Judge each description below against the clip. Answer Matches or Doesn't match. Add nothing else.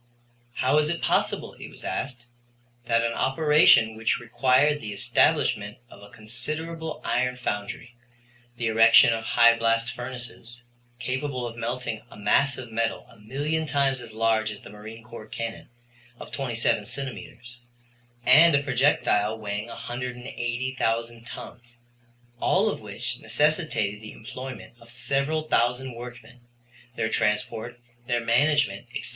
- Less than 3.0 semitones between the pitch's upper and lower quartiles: Matches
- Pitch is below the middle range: Matches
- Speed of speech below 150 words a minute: Matches